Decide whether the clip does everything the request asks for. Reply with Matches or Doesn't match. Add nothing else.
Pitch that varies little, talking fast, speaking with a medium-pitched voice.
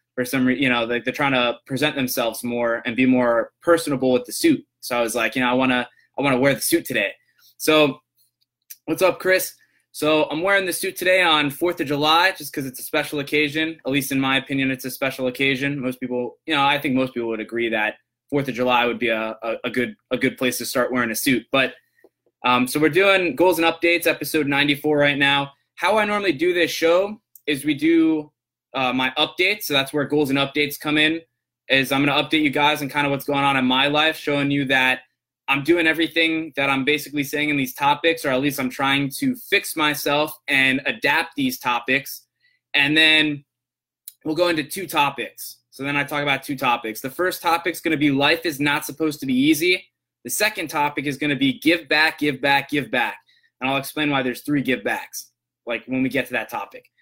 Doesn't match